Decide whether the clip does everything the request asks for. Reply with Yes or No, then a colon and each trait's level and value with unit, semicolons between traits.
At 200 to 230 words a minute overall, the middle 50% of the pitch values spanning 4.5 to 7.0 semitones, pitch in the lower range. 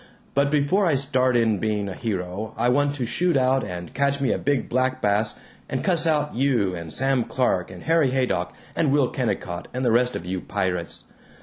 Yes: fast, 205 wpm; wide, 5.5 semitones; low, 125 Hz